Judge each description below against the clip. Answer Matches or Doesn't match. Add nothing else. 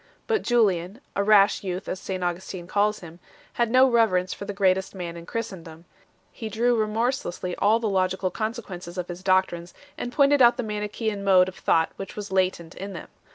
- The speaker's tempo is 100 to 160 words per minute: Doesn't match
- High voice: Matches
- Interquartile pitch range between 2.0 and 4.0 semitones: Matches